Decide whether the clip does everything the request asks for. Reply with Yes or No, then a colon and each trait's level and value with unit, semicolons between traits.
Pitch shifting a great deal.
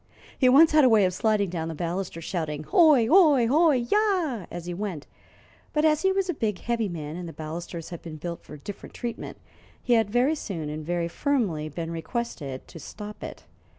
Yes: wide, 7.9 semitones